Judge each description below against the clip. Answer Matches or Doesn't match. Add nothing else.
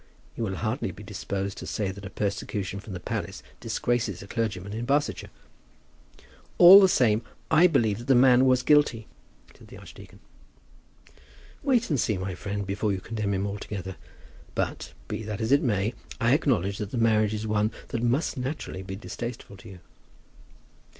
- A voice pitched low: Matches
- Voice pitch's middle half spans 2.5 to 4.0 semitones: Matches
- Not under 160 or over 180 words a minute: Matches